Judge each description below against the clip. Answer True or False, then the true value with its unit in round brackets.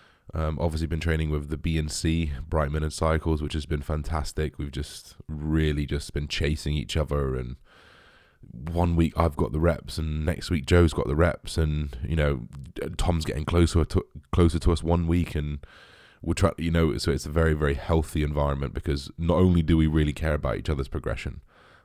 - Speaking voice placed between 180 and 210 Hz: False (80 Hz)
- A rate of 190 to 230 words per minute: True (205 wpm)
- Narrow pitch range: True (2.2 semitones)